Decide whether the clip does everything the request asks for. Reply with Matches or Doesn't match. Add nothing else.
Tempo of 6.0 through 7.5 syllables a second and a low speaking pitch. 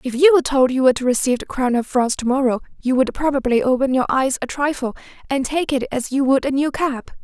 Doesn't match